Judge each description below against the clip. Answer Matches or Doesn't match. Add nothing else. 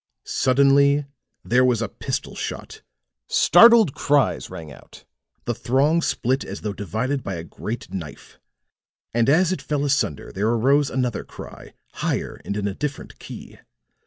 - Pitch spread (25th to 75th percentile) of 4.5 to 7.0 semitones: Matches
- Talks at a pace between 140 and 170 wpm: Matches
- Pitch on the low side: Matches